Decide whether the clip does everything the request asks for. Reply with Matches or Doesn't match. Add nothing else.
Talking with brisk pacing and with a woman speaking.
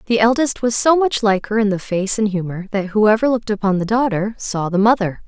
Matches